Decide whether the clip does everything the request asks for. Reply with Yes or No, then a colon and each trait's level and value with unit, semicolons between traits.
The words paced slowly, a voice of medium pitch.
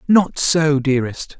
Yes: slow, 130 wpm; medium, 150 Hz